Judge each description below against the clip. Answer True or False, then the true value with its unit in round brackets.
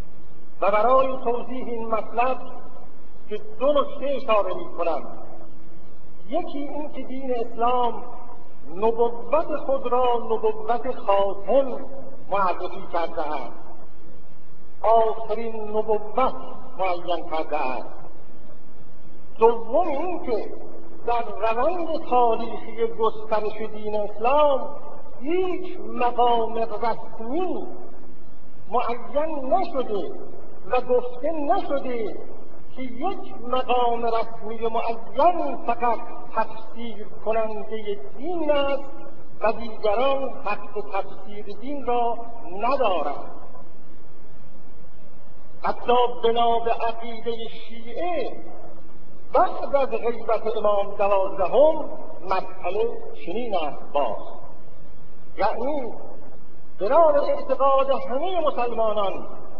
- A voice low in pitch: False (235 Hz)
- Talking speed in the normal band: False (80 wpm)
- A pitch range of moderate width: True (3.9 semitones)